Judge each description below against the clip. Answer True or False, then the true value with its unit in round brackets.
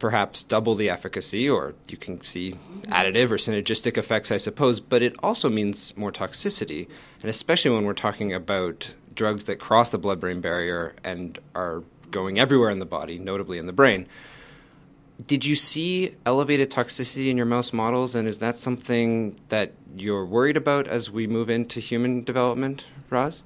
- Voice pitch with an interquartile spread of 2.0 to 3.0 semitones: False (4.8 semitones)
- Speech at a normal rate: True (175 wpm)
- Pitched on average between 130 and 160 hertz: False (115 Hz)